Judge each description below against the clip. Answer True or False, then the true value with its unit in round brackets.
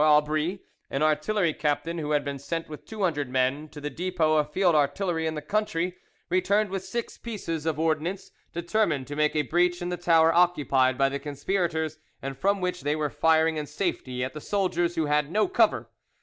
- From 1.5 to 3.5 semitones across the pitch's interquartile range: True (3.2 semitones)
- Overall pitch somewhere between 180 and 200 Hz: False (160 Hz)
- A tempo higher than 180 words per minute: True (200 wpm)